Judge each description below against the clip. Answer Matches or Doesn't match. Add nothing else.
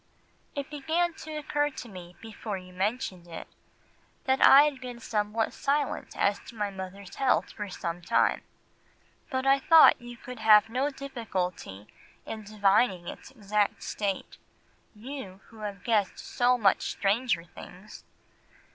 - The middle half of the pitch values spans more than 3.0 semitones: Matches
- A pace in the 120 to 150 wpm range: Matches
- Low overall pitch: Doesn't match